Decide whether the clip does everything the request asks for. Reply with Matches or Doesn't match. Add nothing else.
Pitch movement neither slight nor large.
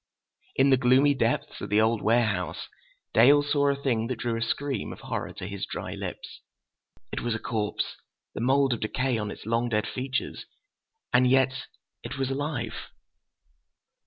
Matches